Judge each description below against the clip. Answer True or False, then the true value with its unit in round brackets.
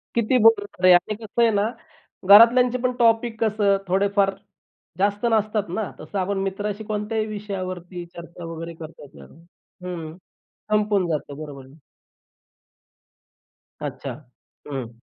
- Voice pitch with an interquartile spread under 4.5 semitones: True (3.7 semitones)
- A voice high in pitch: True (200 Hz)